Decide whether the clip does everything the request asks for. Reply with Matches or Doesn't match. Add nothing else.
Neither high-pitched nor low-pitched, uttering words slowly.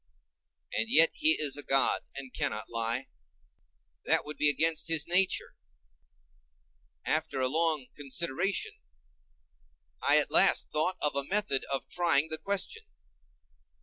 Matches